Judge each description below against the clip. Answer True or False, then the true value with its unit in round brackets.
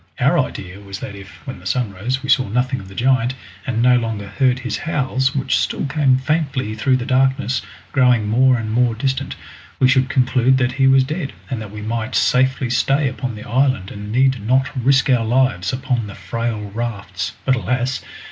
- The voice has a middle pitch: False (125 Hz)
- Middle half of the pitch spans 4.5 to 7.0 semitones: False (3.1 semitones)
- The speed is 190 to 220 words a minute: True (200 wpm)